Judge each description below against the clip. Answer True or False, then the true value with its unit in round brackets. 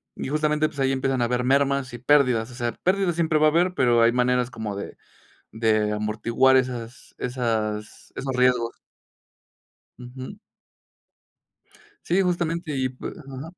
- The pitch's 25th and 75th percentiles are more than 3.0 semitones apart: True (4.0 semitones)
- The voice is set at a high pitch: False (130 Hz)